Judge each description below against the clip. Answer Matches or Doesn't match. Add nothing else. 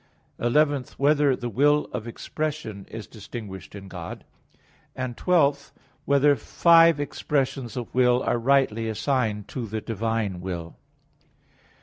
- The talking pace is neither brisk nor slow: Doesn't match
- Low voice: Matches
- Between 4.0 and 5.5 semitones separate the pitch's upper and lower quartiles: Matches